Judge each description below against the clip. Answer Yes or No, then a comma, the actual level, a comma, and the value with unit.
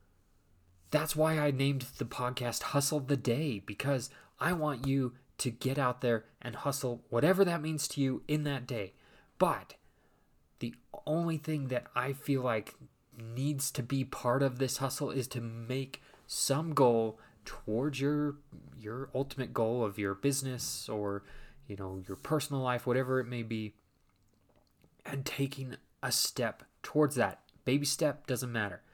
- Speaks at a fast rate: No, average, 155 wpm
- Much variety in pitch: No, average, 3.3 semitones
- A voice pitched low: Yes, low, 130 Hz